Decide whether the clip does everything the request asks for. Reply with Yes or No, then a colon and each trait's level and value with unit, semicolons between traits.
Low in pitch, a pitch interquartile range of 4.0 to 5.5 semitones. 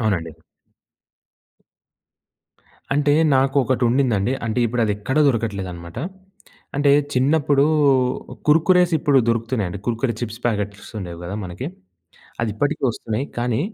Yes: low, 120 Hz; average, 4.8 semitones